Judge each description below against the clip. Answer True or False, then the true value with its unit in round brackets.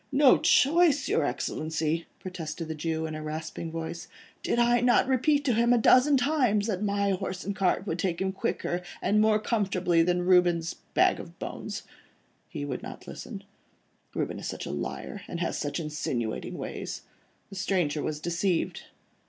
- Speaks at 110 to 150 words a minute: False (170 wpm)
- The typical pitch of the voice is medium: True (180 Hz)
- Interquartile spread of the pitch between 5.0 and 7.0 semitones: True (5.3 semitones)